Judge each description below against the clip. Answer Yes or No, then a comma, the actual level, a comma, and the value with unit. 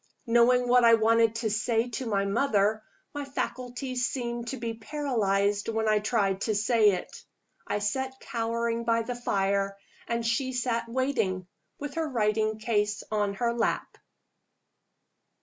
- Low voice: No, high, 230 Hz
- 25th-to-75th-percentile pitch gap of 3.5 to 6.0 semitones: No, average, 2.7 semitones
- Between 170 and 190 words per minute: No, average, 150 wpm